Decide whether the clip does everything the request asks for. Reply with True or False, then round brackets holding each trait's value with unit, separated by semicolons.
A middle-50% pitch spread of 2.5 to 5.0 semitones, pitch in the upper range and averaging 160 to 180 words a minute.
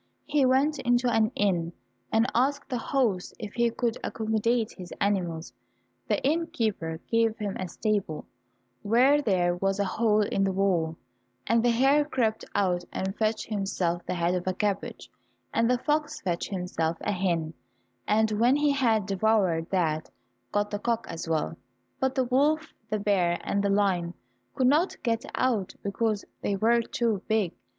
True (4.4 semitones; 215 Hz; 165 wpm)